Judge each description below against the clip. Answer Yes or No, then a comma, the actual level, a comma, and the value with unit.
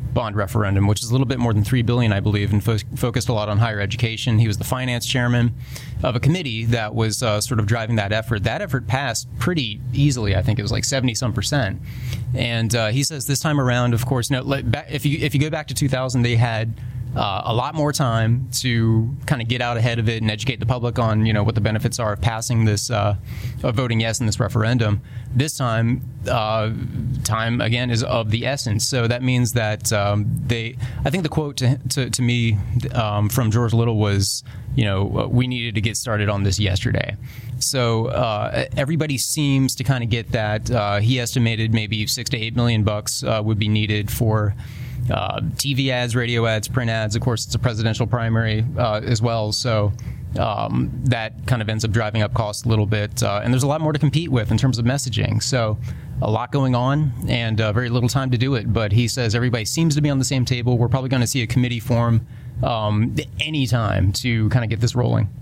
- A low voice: Yes, low, 120 Hz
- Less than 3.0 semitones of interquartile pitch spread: Yes, narrow, 2.4 semitones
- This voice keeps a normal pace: No, fast, 230 wpm